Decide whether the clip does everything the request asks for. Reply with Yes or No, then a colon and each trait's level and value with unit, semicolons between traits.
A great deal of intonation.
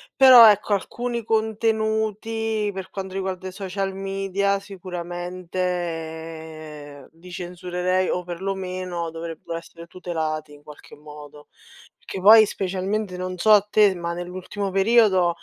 No: average, 2.9 semitones